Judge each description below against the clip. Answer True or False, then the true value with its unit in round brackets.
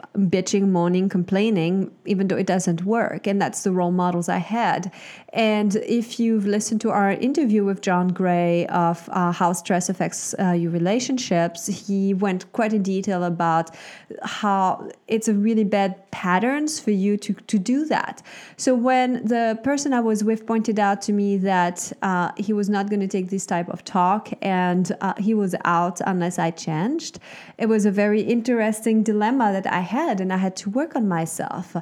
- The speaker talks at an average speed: True (185 wpm)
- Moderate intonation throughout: True (3.4 semitones)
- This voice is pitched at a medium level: False (200 Hz)